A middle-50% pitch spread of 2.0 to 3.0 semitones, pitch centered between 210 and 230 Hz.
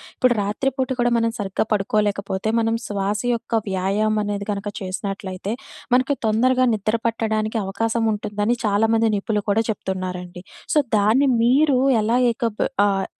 Yes: narrow, 2.4 semitones; high, 215 Hz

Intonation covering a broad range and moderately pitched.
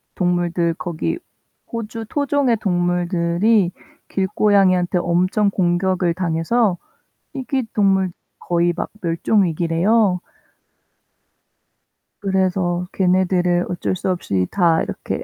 No: narrow, 2.5 semitones; medium, 180 Hz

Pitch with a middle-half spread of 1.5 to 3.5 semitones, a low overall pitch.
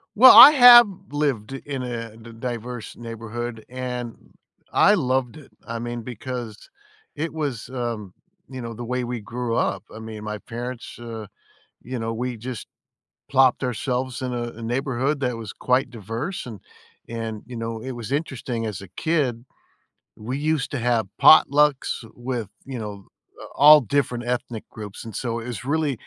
Yes: narrow, 2.6 semitones; low, 120 Hz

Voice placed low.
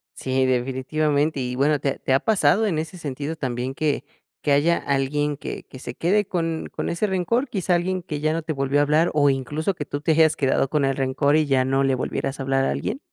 No: medium, 145 Hz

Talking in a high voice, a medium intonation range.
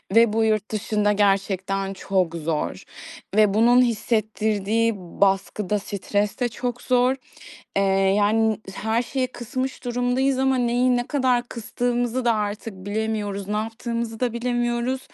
Yes: high, 225 Hz; average, 3.0 semitones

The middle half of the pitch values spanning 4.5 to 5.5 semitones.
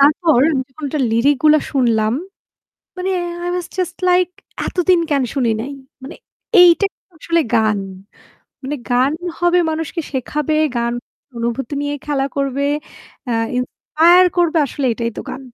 Yes: average, 5.0 semitones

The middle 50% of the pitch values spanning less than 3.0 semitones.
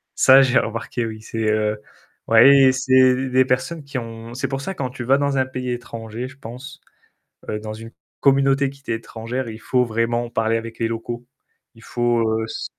Yes: narrow, 2.6 semitones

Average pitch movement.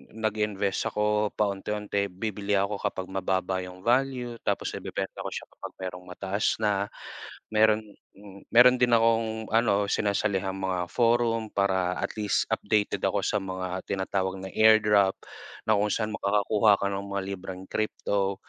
No: narrow, 2.2 semitones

